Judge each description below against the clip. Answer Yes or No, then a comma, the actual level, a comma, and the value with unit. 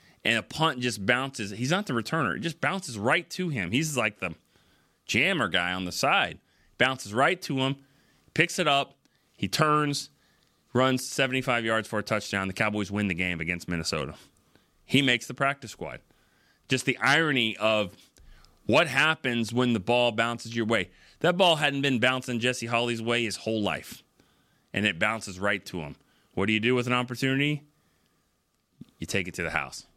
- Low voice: Yes, low, 120 Hz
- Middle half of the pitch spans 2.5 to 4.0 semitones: No, average, 4.7 semitones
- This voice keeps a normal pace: Yes, average, 185 wpm